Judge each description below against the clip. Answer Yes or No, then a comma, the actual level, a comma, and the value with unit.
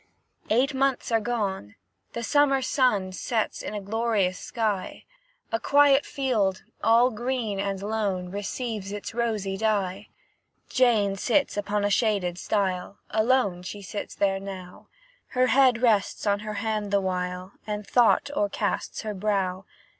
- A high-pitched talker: Yes, high, 210 Hz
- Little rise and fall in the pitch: No, average, 3.5 semitones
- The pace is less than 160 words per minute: Yes, average, 140 wpm